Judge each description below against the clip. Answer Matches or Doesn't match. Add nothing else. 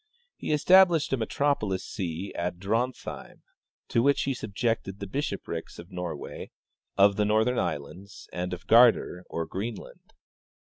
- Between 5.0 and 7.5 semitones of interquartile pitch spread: Matches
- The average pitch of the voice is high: Doesn't match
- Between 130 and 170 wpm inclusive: Matches